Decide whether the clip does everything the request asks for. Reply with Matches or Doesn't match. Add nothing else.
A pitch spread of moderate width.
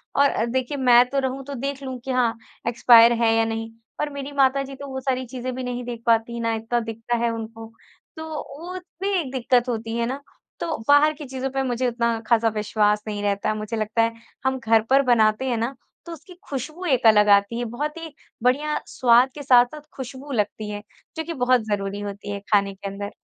Matches